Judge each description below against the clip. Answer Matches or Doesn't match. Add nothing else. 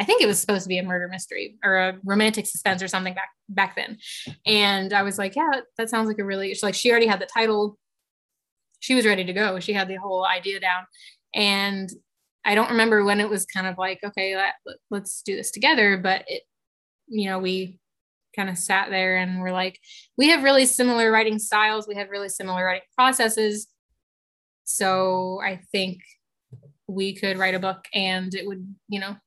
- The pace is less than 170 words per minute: Doesn't match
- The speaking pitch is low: Doesn't match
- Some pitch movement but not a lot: Doesn't match